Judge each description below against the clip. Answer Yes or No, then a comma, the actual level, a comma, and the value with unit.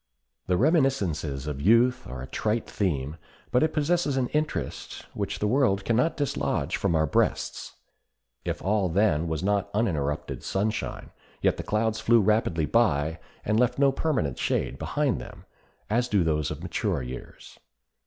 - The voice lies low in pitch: Yes, low, 105 Hz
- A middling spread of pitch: No, wide, 7.6 semitones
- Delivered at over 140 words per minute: Yes, average, 160 wpm